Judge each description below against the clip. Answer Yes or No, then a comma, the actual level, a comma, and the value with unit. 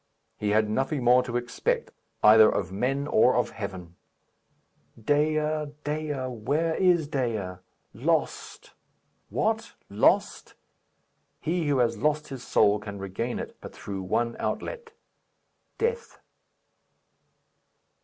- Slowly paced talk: Yes, slow, 115 wpm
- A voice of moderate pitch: No, low, 125 Hz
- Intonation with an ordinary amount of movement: No, wide, 6.1 semitones